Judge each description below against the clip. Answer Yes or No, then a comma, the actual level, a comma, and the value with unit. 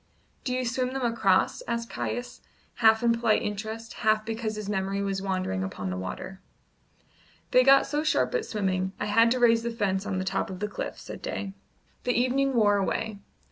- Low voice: No, high, 220 Hz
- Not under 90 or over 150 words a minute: No, average, 195 wpm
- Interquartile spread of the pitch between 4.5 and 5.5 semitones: No, average, 3.6 semitones